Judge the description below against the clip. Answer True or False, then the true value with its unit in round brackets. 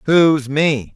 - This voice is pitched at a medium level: True (145 Hz)